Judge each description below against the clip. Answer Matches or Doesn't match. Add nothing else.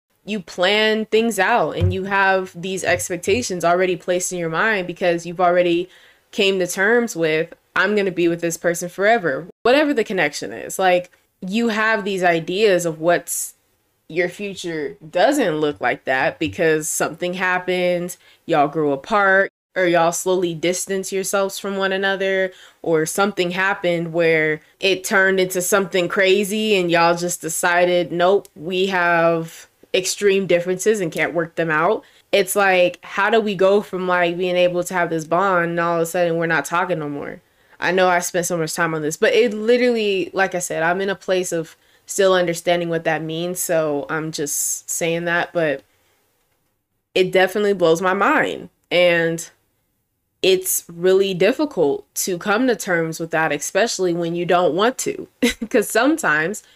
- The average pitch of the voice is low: Doesn't match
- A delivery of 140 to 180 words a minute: Matches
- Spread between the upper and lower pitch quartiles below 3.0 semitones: Matches